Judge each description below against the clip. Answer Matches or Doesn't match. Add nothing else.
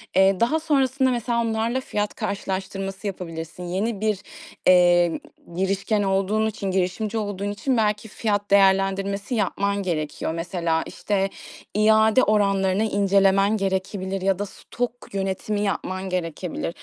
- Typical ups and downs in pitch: Doesn't match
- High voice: Matches